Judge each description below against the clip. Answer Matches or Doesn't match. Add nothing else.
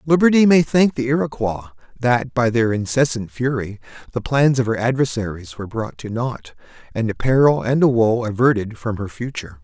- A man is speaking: Matches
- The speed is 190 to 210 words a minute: Doesn't match